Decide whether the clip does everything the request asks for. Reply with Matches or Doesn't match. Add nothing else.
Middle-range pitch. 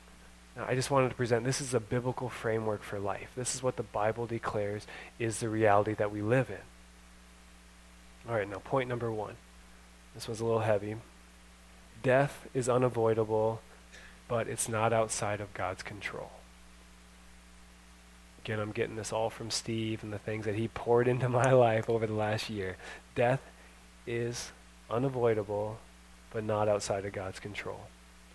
Doesn't match